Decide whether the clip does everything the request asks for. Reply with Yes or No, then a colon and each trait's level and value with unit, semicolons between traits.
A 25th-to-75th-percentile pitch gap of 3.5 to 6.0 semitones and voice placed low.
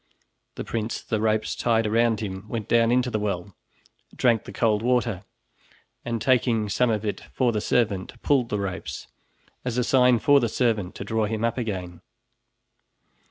No: narrow, 2.4 semitones; low, 115 Hz